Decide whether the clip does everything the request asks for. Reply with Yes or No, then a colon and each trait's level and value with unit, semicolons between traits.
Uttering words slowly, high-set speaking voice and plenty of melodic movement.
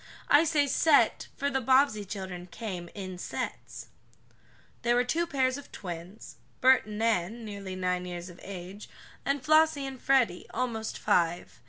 No: average, 155 wpm; high, 220 Hz; wide, 6.7 semitones